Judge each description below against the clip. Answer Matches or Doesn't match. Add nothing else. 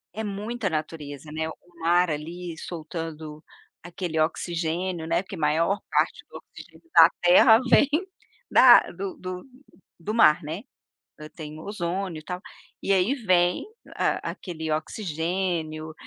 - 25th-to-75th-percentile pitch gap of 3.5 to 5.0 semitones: Doesn't match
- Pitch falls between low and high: Matches